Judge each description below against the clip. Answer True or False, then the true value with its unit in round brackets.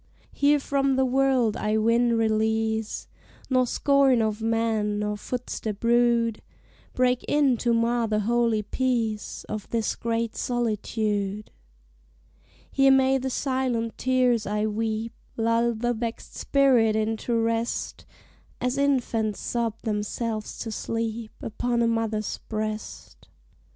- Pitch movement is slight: True (2.2 semitones)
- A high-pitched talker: True (230 Hz)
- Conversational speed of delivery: False (120 wpm)